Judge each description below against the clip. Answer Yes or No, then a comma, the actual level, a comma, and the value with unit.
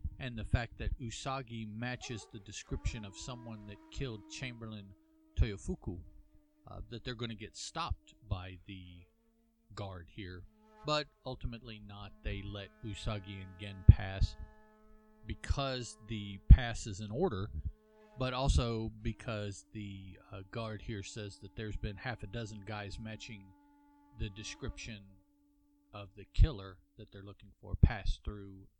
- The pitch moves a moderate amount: Yes, average, 3.3 semitones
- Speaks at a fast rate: No, average, 140 wpm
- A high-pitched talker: No, low, 105 Hz